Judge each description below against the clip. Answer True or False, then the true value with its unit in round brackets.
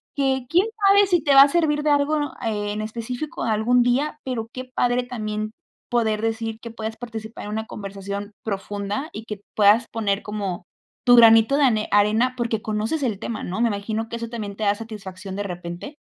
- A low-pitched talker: False (225 Hz)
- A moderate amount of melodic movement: True (3.0 semitones)